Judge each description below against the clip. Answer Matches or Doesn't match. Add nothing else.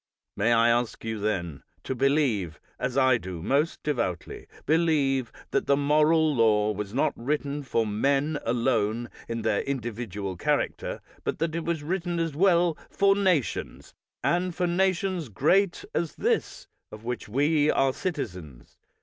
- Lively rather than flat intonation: Matches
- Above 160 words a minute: Doesn't match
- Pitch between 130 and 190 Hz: Matches